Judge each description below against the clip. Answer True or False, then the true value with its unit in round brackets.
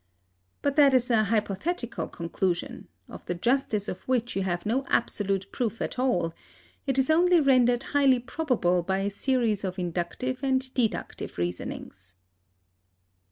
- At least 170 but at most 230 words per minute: False (145 wpm)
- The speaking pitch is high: True (230 Hz)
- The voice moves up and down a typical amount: False (5.7 semitones)